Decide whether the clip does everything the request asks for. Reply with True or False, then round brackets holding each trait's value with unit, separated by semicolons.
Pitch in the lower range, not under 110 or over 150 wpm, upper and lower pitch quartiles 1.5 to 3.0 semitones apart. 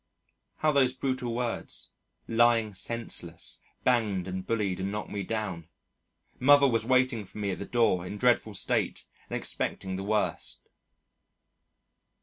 False (110 Hz; 140 wpm; 4.1 semitones)